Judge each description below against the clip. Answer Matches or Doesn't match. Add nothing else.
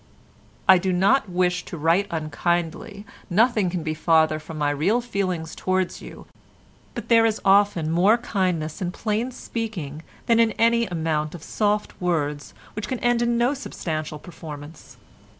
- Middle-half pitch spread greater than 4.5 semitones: Matches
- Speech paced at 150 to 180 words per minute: Matches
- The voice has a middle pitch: Matches